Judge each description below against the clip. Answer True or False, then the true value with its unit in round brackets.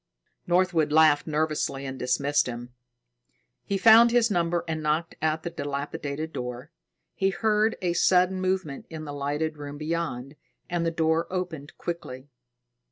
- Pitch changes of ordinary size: True (3.5 semitones)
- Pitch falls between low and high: True (160 Hz)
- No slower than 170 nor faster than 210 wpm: False (145 wpm)